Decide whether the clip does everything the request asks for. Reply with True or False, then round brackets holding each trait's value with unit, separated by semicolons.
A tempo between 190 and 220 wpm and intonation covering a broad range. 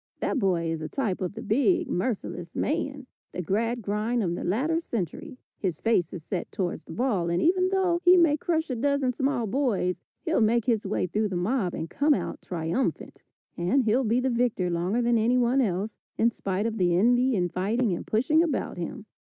True (200 wpm; 6.3 semitones)